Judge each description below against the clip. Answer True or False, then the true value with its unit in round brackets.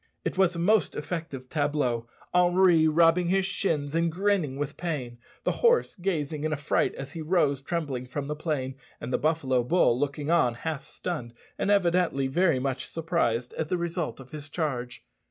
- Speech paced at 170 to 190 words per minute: True (175 wpm)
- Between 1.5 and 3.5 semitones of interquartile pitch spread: False (4.1 semitones)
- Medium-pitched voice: True (155 Hz)